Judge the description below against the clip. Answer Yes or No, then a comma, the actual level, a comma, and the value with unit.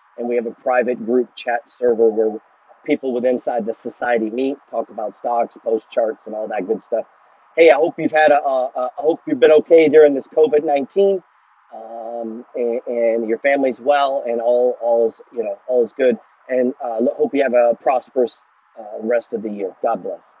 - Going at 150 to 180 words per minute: No, fast, 205 wpm